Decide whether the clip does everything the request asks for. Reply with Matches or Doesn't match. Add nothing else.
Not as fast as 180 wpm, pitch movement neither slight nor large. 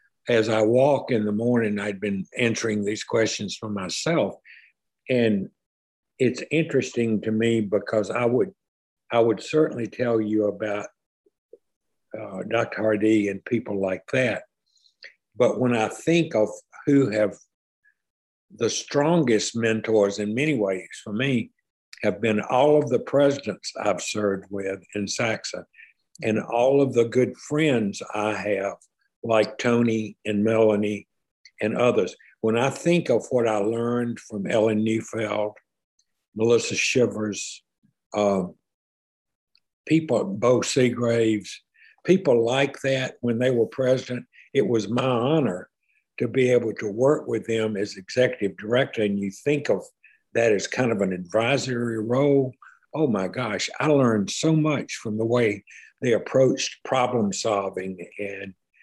Matches